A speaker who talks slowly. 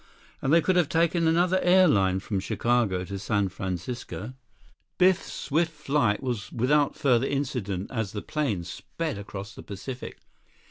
No: average, 145 wpm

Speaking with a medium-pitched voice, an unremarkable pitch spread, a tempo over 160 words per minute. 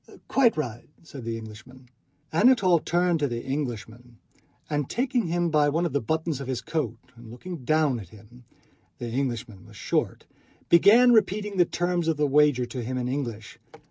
No: medium, 145 Hz; wide, 6.1 semitones; average, 170 wpm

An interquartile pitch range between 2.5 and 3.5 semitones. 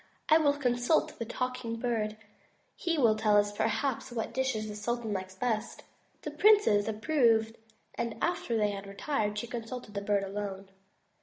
Yes: average, 3.2 semitones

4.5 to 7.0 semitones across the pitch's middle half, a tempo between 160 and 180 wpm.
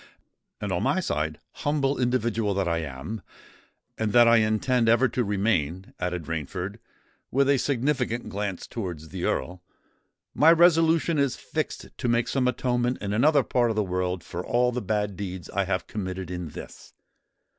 Yes: average, 5.3 semitones; average, 165 wpm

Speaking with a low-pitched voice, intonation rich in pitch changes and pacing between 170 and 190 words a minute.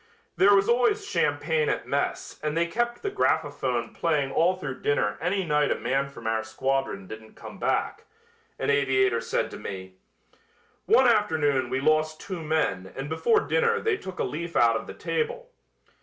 No: medium, 150 Hz; wide, 7.1 semitones; average, 175 wpm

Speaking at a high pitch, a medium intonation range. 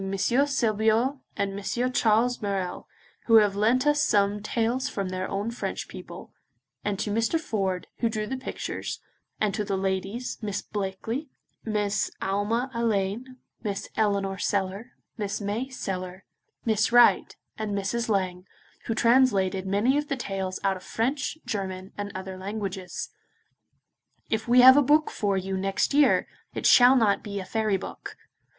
Yes: high, 210 Hz; average, 3.5 semitones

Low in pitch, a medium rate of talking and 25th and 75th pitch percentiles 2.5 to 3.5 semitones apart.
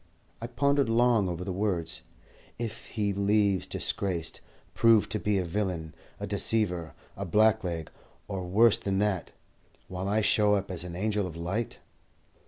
Yes: low, 100 Hz; average, 155 wpm; average, 3.2 semitones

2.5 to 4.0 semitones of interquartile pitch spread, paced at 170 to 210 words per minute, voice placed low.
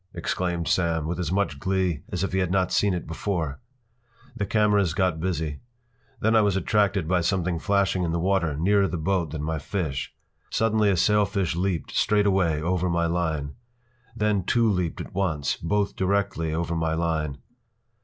Yes: average, 3.4 semitones; average, 175 wpm; very low, 90 Hz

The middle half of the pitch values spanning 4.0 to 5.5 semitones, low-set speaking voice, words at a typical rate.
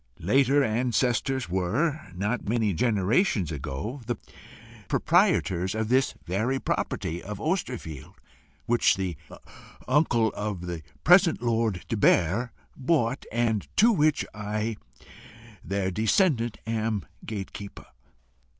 No: average, 5.1 semitones; low, 115 Hz; slow, 110 wpm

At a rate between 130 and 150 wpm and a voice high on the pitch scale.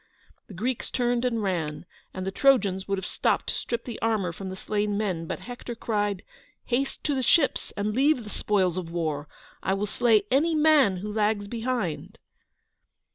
No: average, 185 wpm; high, 210 Hz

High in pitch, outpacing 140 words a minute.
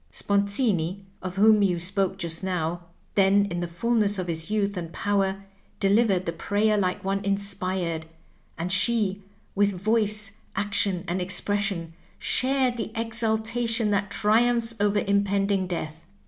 No: high, 200 Hz; slow, 135 wpm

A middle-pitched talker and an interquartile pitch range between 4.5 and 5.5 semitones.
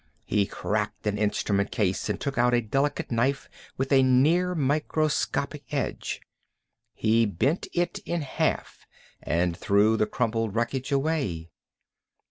No: low, 120 Hz; average, 5.2 semitones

